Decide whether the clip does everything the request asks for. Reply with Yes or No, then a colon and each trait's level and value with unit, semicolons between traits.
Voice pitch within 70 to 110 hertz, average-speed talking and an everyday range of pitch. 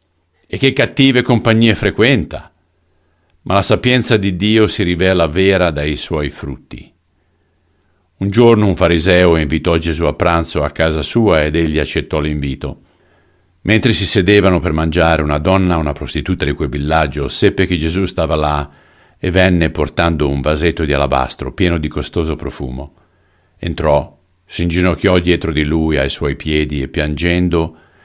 Yes: very low, 85 Hz; average, 150 wpm; average, 3.4 semitones